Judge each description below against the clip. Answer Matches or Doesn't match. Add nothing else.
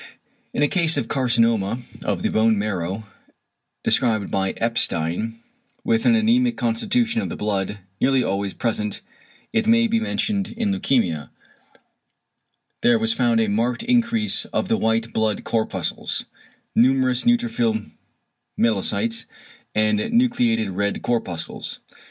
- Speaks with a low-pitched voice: Matches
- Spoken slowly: Matches